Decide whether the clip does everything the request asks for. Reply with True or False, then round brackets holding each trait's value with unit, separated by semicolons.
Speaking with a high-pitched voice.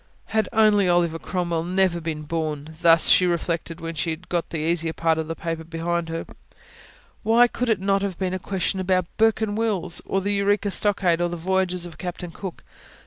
False (175 Hz)